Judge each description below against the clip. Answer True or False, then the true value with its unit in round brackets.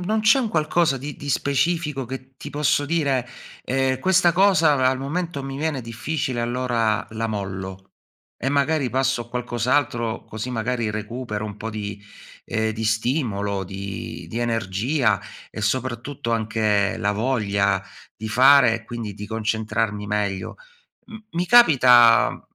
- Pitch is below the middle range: True (120 Hz)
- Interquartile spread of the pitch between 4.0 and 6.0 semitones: True (4.5 semitones)